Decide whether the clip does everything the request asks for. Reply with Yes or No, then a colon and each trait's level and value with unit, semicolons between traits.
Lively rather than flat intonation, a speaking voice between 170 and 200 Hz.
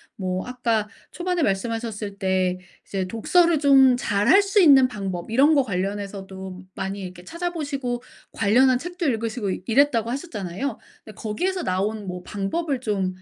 No: wide, 6.2 semitones; high, 225 Hz